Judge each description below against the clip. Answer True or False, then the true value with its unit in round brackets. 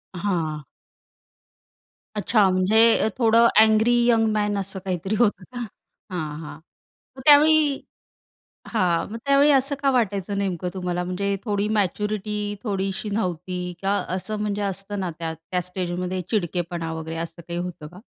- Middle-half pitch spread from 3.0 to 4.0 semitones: True (3.3 semitones)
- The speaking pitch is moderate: False (195 Hz)